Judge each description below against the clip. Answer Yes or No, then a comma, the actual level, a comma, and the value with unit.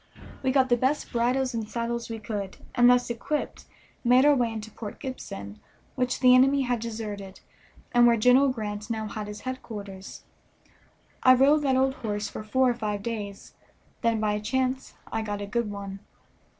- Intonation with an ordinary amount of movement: Yes, average, 3.5 semitones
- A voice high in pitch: Yes, high, 235 Hz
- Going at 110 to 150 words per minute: No, average, 180 wpm